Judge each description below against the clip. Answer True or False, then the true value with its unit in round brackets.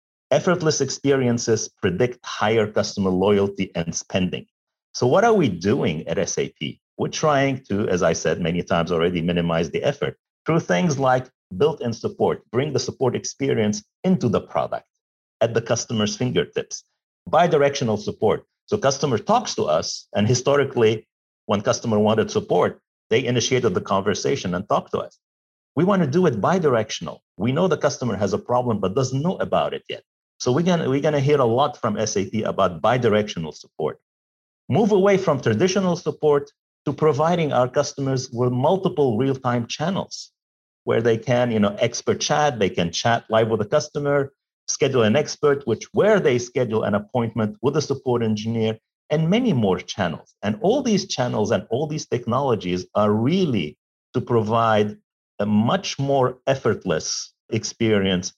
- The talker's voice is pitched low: True (125 Hz)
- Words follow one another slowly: False (160 wpm)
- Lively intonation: True (5.7 semitones)